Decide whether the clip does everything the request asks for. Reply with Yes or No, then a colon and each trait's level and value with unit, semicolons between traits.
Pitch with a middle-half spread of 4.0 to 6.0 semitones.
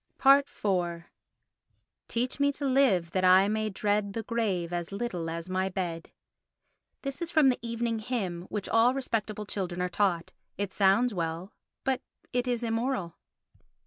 Yes: average, 5.1 semitones